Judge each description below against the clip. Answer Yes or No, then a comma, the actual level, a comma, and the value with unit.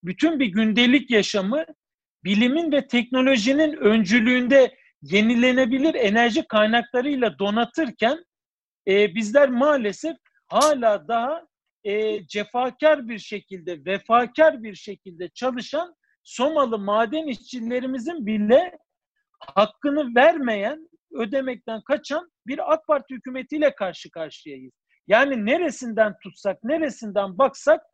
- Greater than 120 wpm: No, slow, 95 wpm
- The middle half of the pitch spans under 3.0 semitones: No, wide, 5.6 semitones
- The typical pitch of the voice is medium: No, high, 245 Hz